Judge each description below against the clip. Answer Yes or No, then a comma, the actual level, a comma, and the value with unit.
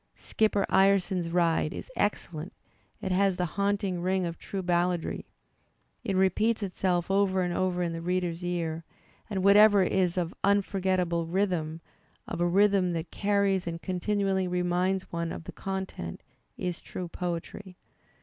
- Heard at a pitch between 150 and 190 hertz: Yes, medium, 185 Hz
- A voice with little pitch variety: Yes, narrow, 2.1 semitones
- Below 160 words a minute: Yes, average, 145 wpm